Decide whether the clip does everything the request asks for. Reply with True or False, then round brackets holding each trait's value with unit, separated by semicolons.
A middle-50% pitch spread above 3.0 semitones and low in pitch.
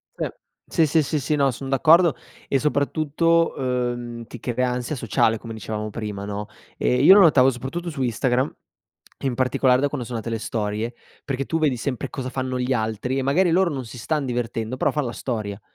True (3.6 semitones; 130 Hz)